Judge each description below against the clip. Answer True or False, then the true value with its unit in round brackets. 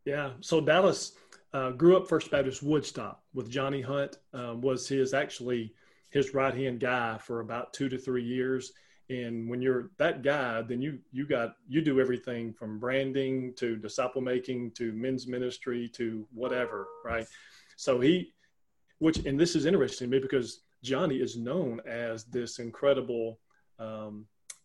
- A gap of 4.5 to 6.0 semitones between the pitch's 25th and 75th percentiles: False (2.5 semitones)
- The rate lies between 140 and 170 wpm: True (160 wpm)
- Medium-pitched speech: False (125 Hz)